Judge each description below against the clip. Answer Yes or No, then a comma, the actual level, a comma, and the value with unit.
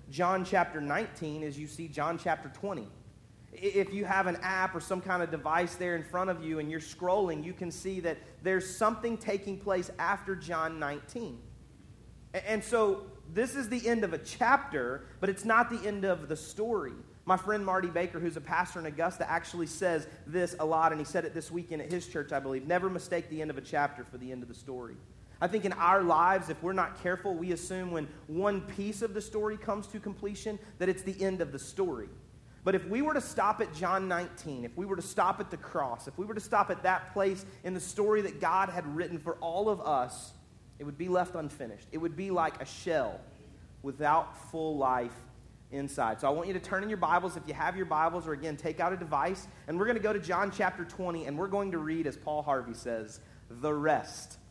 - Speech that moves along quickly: Yes, fast, 230 wpm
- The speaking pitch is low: No, medium, 175 Hz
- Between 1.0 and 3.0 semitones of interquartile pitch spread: No, average, 4.1 semitones